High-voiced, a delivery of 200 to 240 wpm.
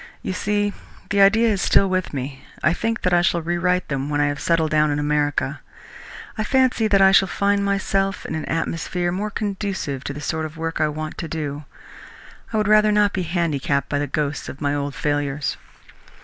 No: medium, 170 Hz; fast, 205 wpm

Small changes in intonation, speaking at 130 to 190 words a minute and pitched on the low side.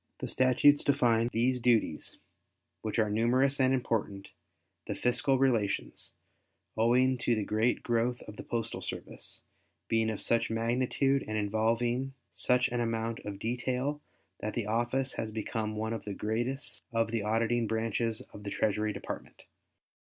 Yes: narrow, 2.2 semitones; average, 150 wpm; low, 115 Hz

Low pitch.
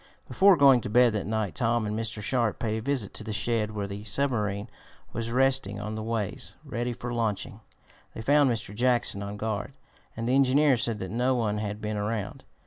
Yes: low, 115 Hz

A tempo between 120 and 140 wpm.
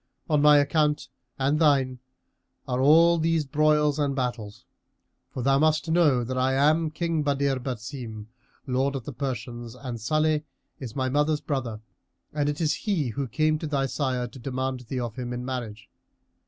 No: average, 170 wpm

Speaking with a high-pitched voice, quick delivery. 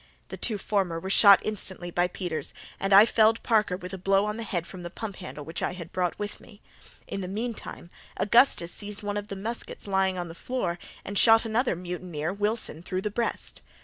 Yes: high, 195 Hz; fast, 210 wpm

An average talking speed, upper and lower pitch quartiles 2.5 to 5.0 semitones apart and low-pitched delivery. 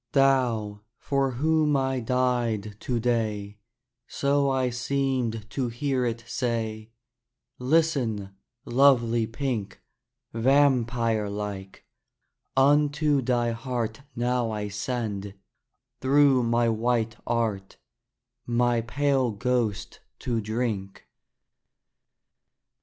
No: slow, 90 wpm; average, 3.2 semitones; low, 120 Hz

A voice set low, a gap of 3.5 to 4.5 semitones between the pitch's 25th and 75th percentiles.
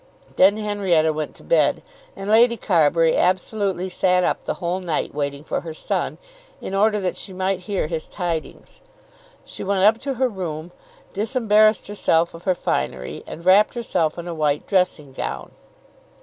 No: medium, 185 Hz; average, 4.0 semitones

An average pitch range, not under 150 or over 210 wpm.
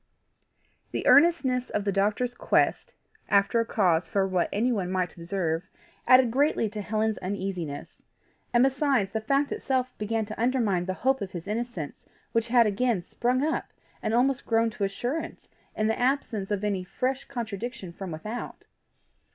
Yes: average, 4.4 semitones; average, 160 wpm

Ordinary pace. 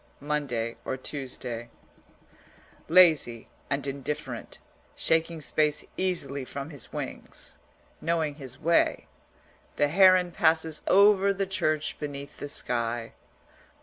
No: slow, 105 wpm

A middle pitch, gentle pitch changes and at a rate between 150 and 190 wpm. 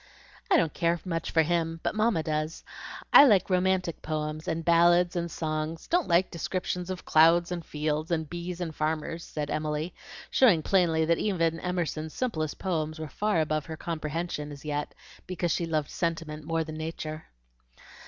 Yes: medium, 165 Hz; narrow, 2.1 semitones; average, 170 wpm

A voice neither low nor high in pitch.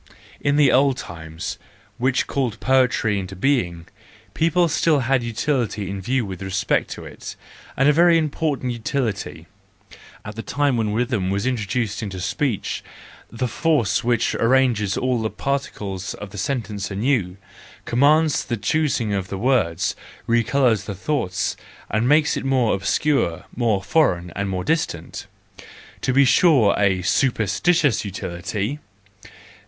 No: low, 115 Hz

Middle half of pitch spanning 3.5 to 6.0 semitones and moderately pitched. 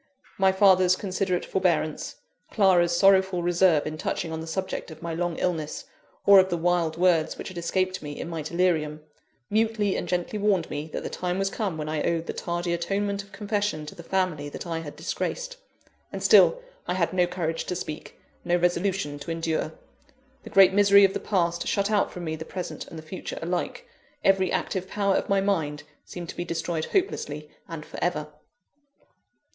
No: average, 3.0 semitones; medium, 175 Hz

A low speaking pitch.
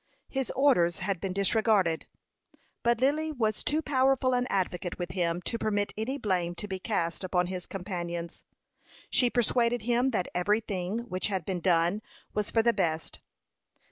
No: high, 200 Hz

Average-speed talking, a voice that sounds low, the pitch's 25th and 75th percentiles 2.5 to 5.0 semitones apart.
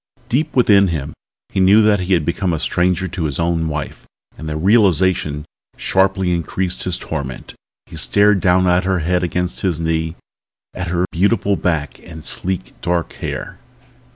Yes: average, 165 wpm; very low, 90 Hz; average, 2.8 semitones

